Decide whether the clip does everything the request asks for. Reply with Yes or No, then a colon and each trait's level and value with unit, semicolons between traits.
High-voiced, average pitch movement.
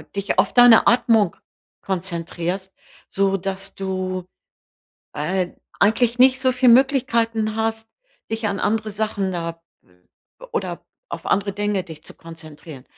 Yes: high, 200 Hz; average, 3.4 semitones